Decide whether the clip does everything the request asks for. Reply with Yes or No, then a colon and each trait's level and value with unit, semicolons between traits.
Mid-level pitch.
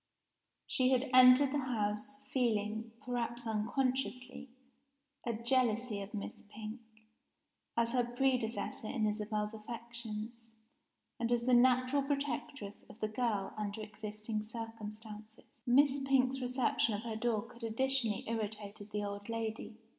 No: high, 230 Hz